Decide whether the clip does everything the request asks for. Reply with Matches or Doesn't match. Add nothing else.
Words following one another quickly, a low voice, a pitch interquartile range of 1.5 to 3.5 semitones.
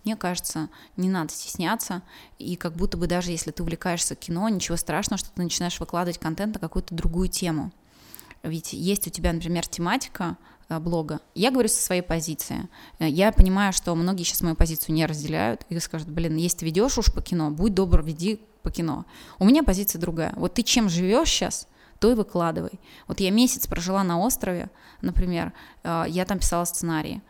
Doesn't match